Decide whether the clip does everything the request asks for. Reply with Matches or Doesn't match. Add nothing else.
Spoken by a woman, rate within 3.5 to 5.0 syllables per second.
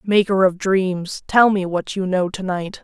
Matches